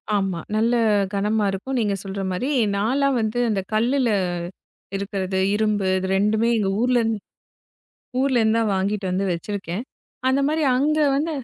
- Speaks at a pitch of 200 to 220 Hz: Yes, high, 215 Hz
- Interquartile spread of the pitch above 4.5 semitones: No, average, 3.8 semitones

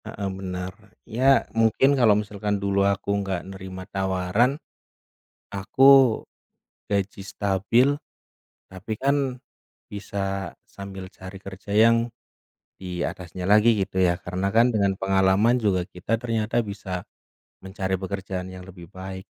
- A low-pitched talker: Yes, low, 100 Hz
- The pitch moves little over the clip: Yes, narrow, 2.3 semitones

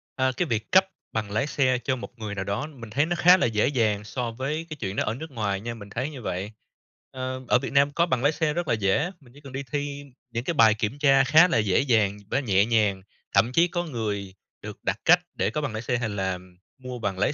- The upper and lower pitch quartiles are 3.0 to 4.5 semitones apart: No, wide, 5.4 semitones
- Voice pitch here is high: No, low, 125 Hz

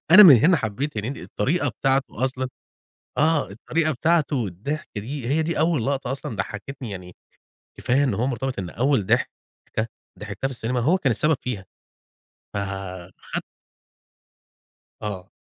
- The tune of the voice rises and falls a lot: Yes, wide, 5.8 semitones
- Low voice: Yes, low, 130 Hz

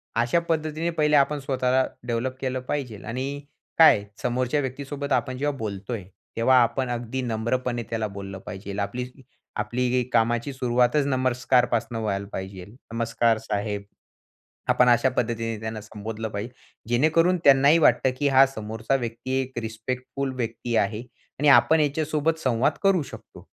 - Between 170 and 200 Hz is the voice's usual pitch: No, low, 125 Hz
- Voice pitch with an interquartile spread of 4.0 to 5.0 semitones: No, average, 3.4 semitones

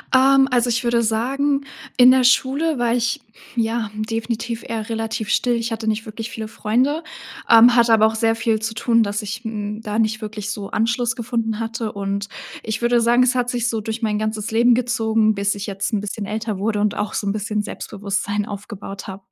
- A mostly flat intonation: Yes, narrow, 2.1 semitones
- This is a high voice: Yes, high, 225 Hz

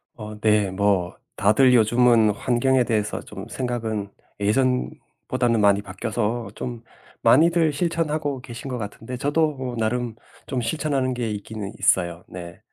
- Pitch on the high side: No, low, 120 Hz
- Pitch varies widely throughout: No, average, 3.6 semitones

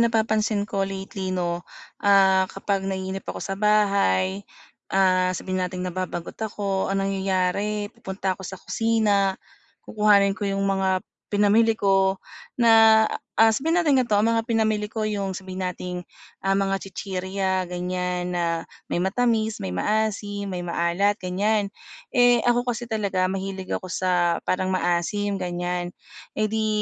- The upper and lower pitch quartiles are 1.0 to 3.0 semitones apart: Yes, narrow, 2.4 semitones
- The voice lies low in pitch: No, high, 195 Hz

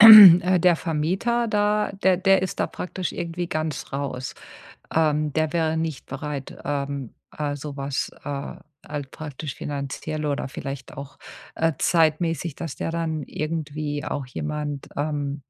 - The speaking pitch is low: No, medium, 155 Hz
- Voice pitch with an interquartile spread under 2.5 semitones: No, average, 2.8 semitones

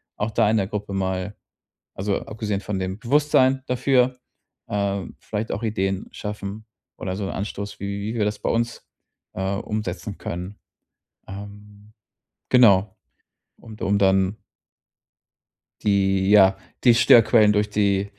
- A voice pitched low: Yes, low, 105 Hz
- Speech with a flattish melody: Yes, narrow, 2.1 semitones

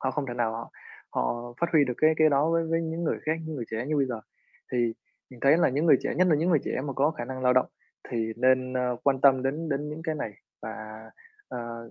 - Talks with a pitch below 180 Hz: Yes, low, 135 Hz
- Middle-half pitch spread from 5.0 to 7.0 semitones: No, average, 4.2 semitones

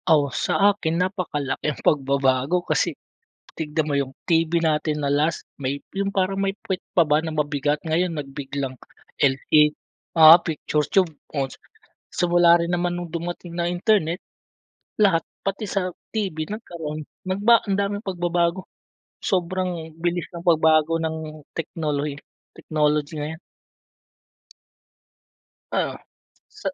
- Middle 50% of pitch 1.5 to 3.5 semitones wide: Yes, average, 3.0 semitones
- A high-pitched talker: No, medium, 165 Hz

